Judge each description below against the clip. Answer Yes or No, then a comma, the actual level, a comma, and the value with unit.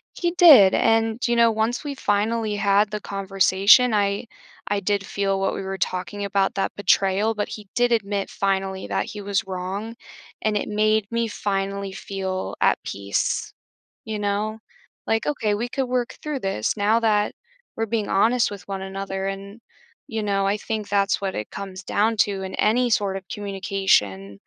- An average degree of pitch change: No, narrow, 2.3 semitones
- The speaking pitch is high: Yes, high, 205 Hz